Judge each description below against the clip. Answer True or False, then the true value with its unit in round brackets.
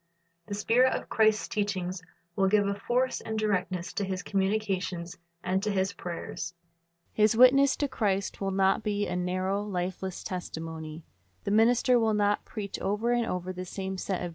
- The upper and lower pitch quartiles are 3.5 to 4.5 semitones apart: False (2.7 semitones)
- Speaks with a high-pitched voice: True (195 Hz)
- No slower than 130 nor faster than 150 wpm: False (170 wpm)